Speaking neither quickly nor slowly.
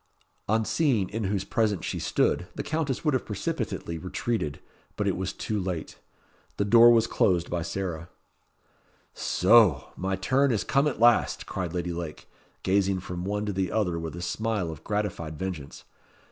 Yes: average, 170 wpm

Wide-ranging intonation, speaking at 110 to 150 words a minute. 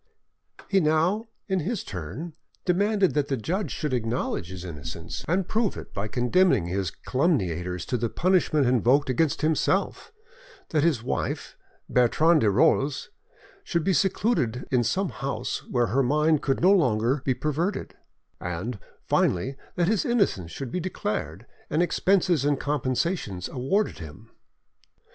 Yes: wide, 7.7 semitones; average, 145 wpm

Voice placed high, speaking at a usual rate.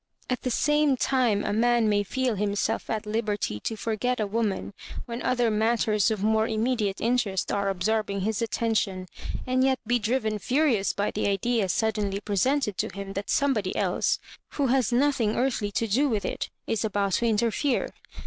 Yes: high, 220 Hz; average, 175 wpm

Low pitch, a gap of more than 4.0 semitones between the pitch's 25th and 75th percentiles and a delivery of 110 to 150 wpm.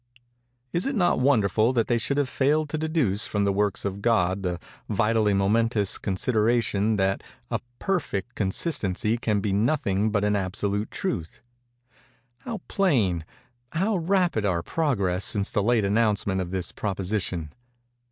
Yes: low, 105 Hz; average, 4.6 semitones; average, 140 wpm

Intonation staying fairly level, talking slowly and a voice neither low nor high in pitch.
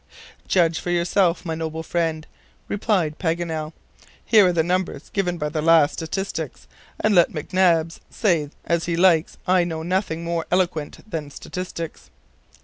No: narrow, 2.1 semitones; average, 145 wpm; medium, 170 Hz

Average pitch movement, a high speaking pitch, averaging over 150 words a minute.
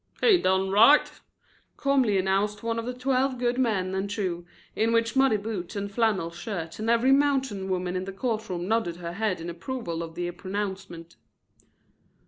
Yes: average, 4.2 semitones; high, 205 Hz; average, 175 wpm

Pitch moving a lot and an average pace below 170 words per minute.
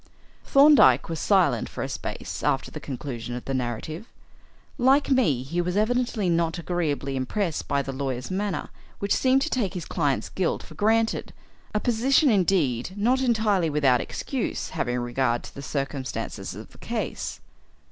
Yes: wide, 8.2 semitones; average, 160 wpm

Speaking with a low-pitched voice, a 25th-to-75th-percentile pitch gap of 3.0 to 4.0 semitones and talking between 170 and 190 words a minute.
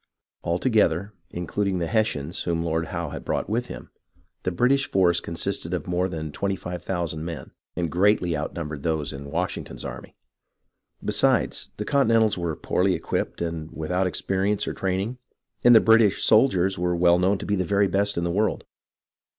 Yes: very low, 90 Hz; average, 3.4 semitones; average, 175 wpm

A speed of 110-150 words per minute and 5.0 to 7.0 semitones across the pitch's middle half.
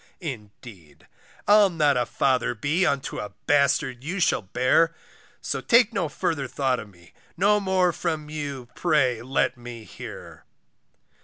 Yes: average, 145 wpm; wide, 5.4 semitones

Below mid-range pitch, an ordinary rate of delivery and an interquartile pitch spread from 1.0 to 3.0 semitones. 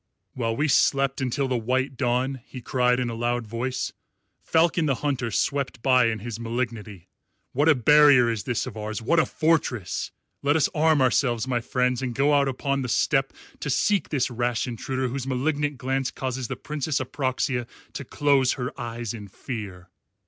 Yes: low, 130 Hz; average, 180 wpm; average, 2.7 semitones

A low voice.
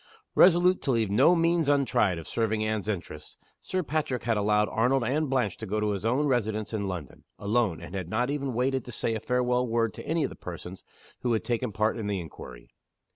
Yes: low, 115 Hz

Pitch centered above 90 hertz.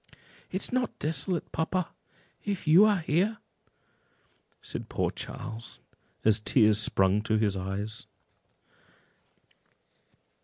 Yes: low, 135 Hz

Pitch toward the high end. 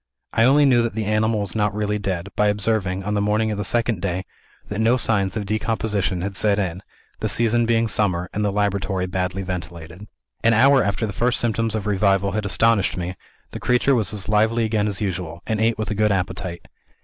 No: low, 105 Hz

